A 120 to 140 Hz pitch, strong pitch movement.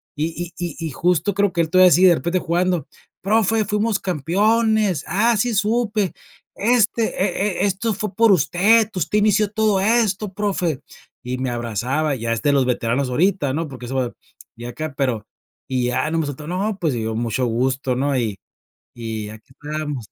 No: medium, 170 Hz; wide, 7.7 semitones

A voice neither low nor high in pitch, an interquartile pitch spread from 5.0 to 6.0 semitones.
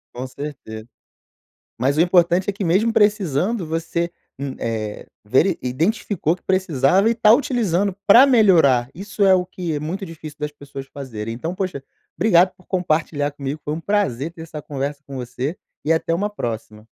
Yes: medium, 165 Hz; wide, 5.6 semitones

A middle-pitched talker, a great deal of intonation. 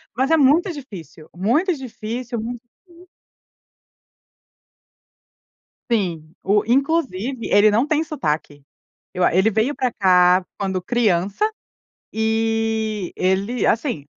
No: high, 220 Hz; wide, 5.7 semitones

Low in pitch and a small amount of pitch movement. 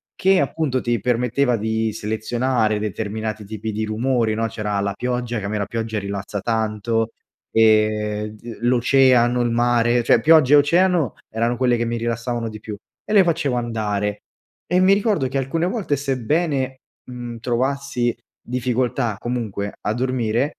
No: low, 120 Hz; average, 3.1 semitones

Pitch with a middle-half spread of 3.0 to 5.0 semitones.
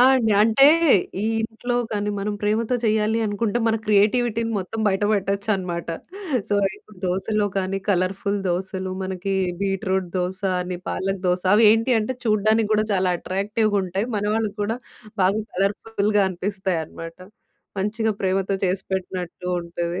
No: narrow, 2.5 semitones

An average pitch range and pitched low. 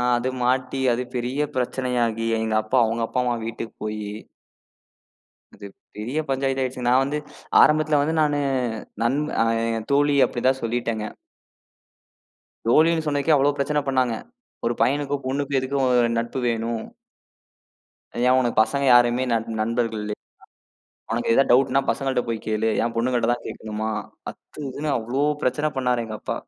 Yes: average, 3.0 semitones; low, 125 Hz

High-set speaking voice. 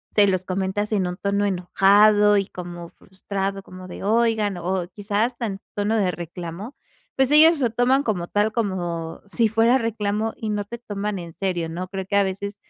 Yes: high, 200 Hz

